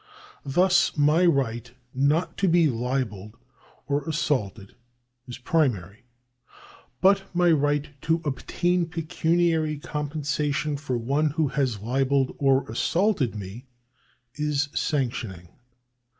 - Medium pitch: Yes, medium, 145 Hz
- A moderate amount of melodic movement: Yes, average, 4.5 semitones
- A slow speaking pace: Yes, slow, 105 wpm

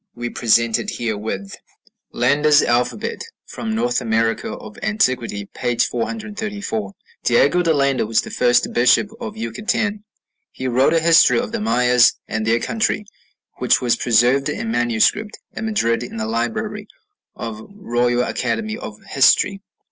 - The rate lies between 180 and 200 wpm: No, average, 150 wpm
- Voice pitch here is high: No, low, 125 Hz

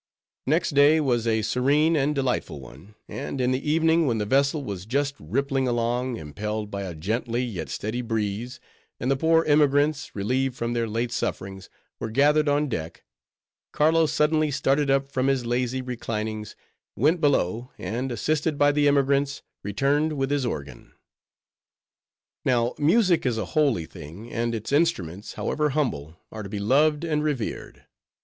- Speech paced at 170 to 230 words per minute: No, average, 160 wpm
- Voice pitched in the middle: No, low, 130 Hz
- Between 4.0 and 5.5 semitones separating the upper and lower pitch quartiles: Yes, average, 4.8 semitones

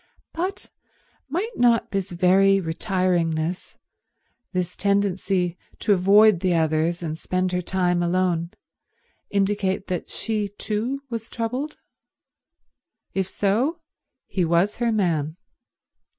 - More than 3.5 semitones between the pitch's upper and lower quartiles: No, average, 3.2 semitones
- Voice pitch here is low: No, high, 190 Hz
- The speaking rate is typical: No, slow, 105 wpm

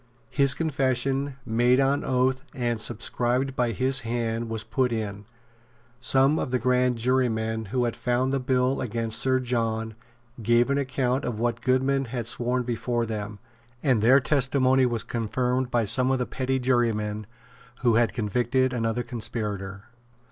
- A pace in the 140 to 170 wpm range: Yes, average, 155 wpm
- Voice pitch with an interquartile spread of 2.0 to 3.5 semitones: Yes, narrow, 2.5 semitones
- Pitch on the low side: Yes, low, 125 Hz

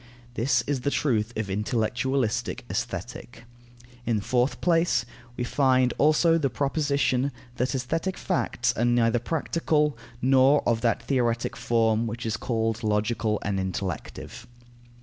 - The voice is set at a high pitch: No, low, 120 Hz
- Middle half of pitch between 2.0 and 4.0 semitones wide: Yes, average, 3.6 semitones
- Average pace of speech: No, slow, 130 wpm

